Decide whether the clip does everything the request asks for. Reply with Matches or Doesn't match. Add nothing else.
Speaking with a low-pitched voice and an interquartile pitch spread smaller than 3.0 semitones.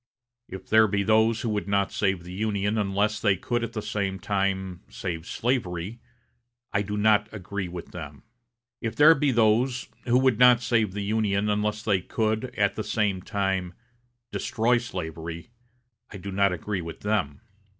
Matches